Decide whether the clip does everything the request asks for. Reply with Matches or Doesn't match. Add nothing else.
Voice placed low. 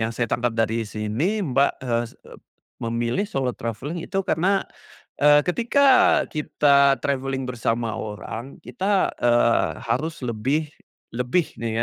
Matches